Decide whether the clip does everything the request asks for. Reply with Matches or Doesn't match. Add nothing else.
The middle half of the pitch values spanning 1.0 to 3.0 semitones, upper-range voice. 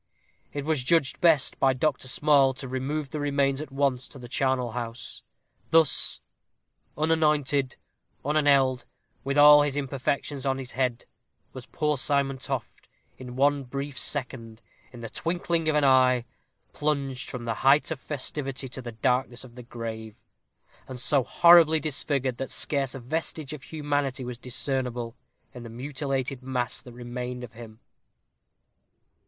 Doesn't match